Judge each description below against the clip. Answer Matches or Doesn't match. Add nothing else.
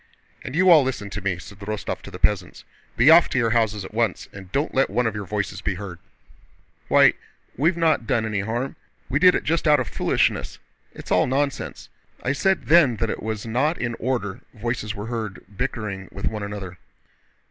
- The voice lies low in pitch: Matches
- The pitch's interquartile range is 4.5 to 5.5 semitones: Matches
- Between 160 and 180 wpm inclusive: Doesn't match